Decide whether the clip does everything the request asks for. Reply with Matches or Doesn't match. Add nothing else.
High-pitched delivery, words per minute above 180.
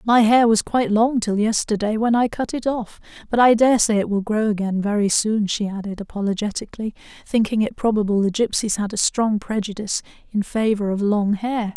Matches